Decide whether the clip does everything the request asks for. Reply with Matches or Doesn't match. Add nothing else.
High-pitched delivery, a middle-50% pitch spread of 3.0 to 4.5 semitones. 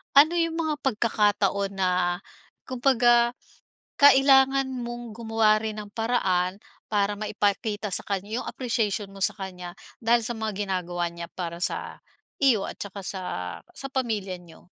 Matches